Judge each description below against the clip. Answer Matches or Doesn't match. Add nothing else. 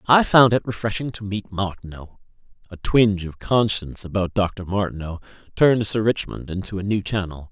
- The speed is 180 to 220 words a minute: Doesn't match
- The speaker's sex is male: Matches